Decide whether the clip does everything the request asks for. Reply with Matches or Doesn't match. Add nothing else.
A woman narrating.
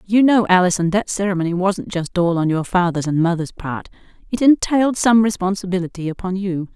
Matches